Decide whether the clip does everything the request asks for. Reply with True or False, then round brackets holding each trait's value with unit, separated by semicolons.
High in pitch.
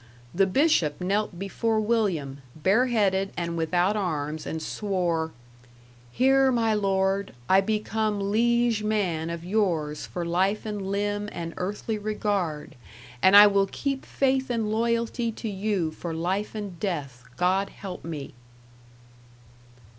True (195 Hz)